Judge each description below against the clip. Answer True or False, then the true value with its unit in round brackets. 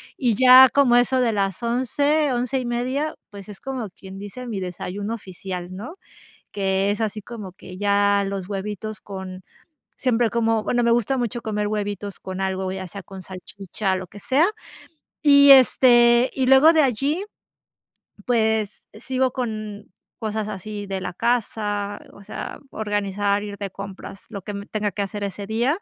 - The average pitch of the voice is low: False (210 Hz)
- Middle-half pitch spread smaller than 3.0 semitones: False (3.6 semitones)